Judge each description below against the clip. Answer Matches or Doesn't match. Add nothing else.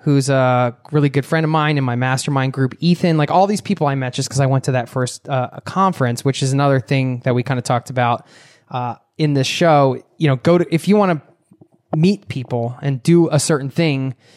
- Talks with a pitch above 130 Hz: Matches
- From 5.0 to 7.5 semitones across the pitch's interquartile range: Doesn't match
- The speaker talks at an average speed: Doesn't match